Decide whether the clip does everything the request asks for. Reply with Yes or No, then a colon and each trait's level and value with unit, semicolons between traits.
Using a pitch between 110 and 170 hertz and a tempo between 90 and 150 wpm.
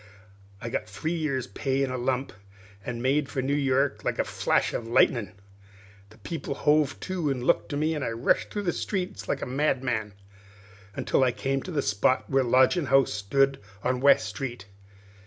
No: low, 135 Hz; average, 195 wpm